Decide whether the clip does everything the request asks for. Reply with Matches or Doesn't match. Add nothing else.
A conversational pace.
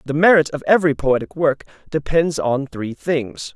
Matches